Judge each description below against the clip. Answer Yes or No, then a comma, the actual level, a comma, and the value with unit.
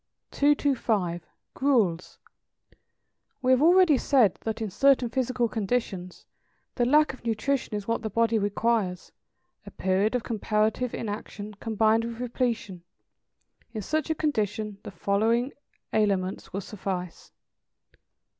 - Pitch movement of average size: Yes, average, 3.8 semitones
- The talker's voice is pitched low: No, high, 225 Hz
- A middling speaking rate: No, slow, 120 wpm